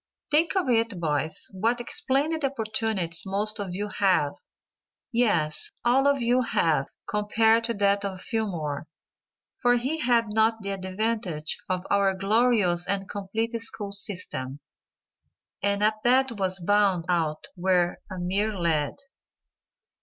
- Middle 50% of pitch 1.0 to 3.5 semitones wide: No, average, 4.0 semitones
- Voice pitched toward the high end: Yes, high, 205 Hz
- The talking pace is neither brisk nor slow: No, slow, 130 wpm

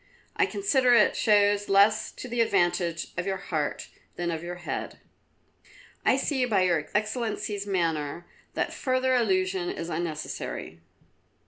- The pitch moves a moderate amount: Yes, average, 4.3 semitones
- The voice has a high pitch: Yes, high, 195 Hz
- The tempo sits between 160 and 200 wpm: No, slow, 135 wpm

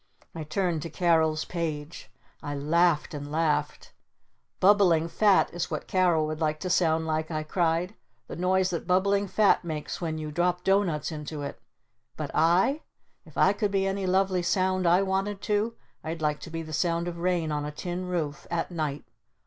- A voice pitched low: No, medium, 170 Hz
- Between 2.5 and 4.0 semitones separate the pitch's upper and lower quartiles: Yes, average, 3.0 semitones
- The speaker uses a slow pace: No, average, 180 wpm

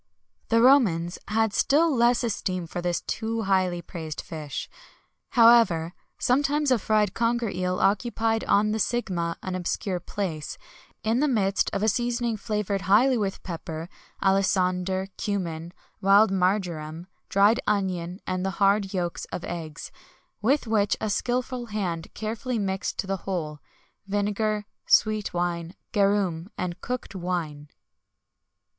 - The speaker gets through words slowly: Yes, slow, 130 wpm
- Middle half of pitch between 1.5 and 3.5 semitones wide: No, average, 3.9 semitones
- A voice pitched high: Yes, high, 195 Hz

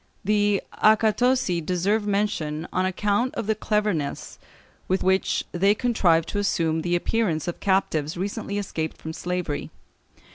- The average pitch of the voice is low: No, high, 190 Hz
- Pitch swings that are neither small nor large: Yes, average, 3.8 semitones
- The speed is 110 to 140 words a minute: Yes, slow, 135 wpm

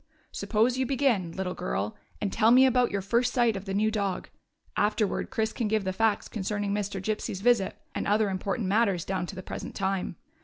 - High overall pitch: Yes, high, 205 Hz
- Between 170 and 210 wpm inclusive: Yes, average, 200 wpm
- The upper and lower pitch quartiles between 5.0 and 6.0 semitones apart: No, average, 2.8 semitones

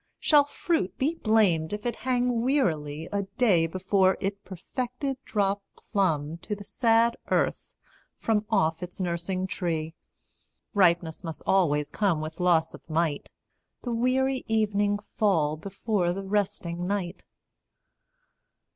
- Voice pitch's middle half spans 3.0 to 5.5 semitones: Yes, average, 4.8 semitones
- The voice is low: No, high, 195 Hz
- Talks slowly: Yes, slow, 130 wpm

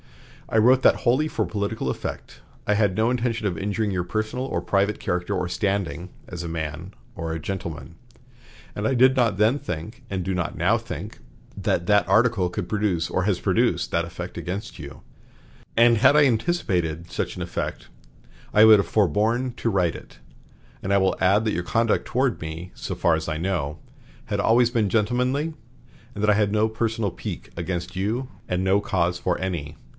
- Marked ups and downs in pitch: No, average, 4.3 semitones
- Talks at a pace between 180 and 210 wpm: Yes, average, 190 wpm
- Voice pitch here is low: Yes, low, 100 Hz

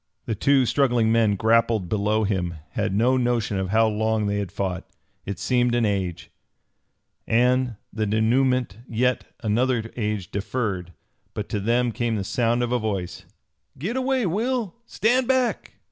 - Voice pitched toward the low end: Yes, low, 115 Hz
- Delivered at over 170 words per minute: No, average, 155 wpm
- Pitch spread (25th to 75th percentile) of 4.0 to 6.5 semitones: No, average, 3.5 semitones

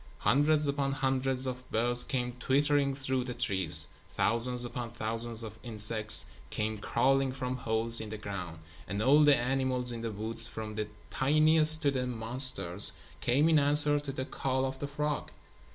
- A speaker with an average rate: Yes, average, 170 wpm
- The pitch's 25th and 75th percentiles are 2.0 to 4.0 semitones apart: Yes, average, 3.5 semitones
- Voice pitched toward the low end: Yes, low, 125 Hz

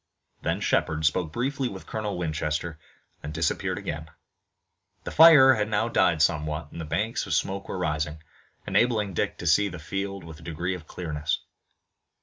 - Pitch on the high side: No, very low, 85 Hz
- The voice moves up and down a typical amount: Yes, average, 4.8 semitones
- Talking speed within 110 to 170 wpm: Yes, average, 165 wpm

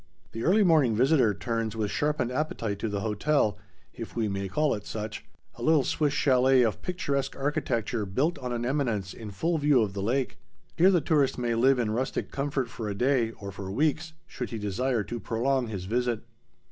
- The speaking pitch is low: Yes, low, 125 Hz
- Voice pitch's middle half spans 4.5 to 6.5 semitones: Yes, average, 4.8 semitones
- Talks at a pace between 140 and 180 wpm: No, average, 195 wpm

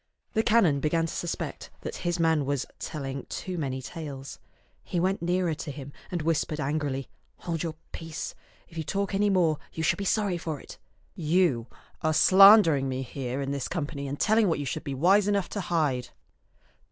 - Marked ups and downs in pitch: No, average, 4.4 semitones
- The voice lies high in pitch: No, medium, 160 Hz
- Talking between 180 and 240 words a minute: Yes, average, 190 wpm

